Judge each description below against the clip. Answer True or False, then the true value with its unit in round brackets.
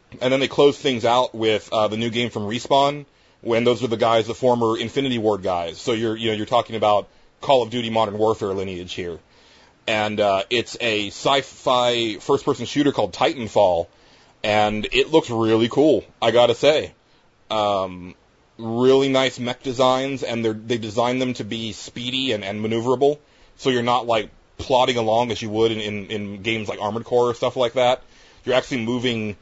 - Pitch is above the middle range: False (115 Hz)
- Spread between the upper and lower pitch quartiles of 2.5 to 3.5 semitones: True (2.8 semitones)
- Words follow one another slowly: False (195 wpm)